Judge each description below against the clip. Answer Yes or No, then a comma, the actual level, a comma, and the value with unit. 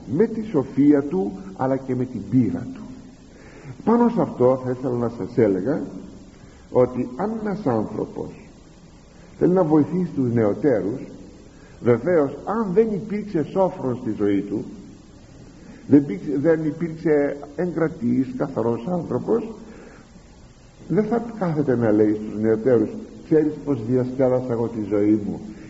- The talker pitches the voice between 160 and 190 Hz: No, medium, 140 Hz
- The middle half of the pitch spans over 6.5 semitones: Yes, wide, 7.6 semitones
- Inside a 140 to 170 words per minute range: No, average, 130 wpm